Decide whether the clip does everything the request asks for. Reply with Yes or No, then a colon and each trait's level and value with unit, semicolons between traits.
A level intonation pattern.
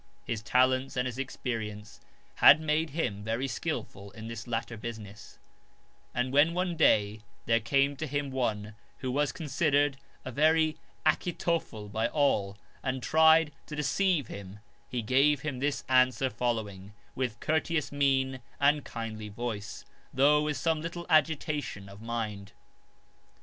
No: average, 5.2 semitones